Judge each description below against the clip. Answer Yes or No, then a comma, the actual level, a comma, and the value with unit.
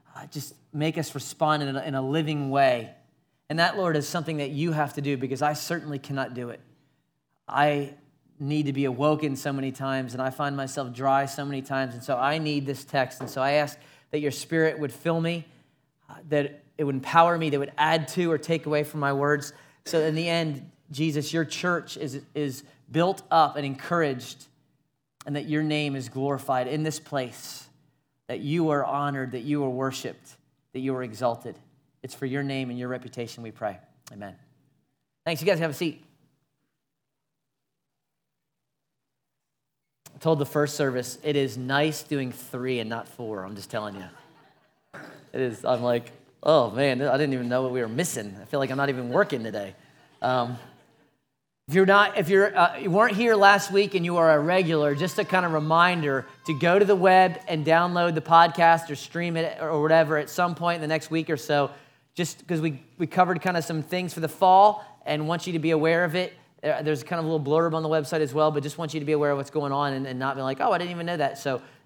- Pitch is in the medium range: Yes, medium, 150 Hz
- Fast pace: Yes, fast, 220 wpm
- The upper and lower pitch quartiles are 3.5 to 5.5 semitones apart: No, average, 3.0 semitones